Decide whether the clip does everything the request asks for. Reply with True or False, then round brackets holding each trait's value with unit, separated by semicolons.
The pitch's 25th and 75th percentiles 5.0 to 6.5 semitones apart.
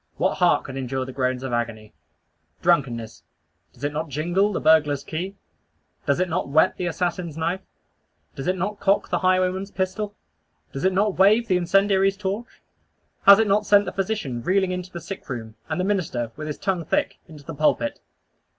True (5.4 semitones)